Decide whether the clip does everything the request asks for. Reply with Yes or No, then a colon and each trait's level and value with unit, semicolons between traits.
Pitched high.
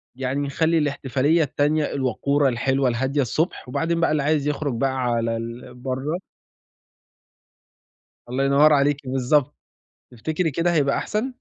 No: medium, 140 Hz